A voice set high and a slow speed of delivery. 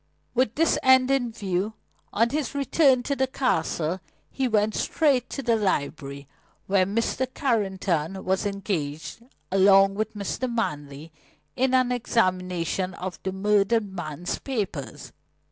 Yes: high, 205 Hz; slow, 130 wpm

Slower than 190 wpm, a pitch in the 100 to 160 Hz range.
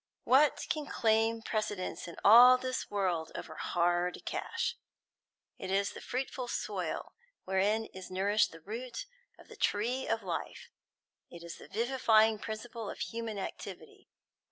No: average, 140 wpm; high, 220 Hz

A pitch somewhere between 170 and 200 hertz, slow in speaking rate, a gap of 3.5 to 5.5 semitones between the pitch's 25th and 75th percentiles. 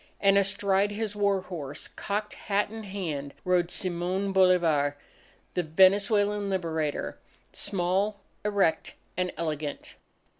No: high, 190 Hz; slow, 110 wpm; average, 3.0 semitones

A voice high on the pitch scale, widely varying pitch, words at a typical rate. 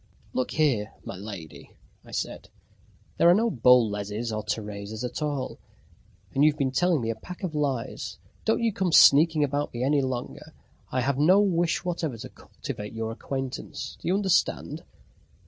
No: low, 135 Hz; wide, 6.3 semitones; average, 165 wpm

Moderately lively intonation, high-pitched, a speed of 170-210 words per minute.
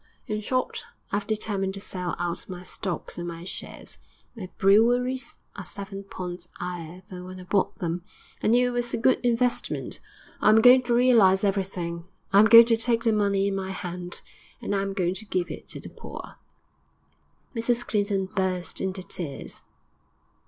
Yes: average, 3.8 semitones; high, 195 Hz; average, 180 wpm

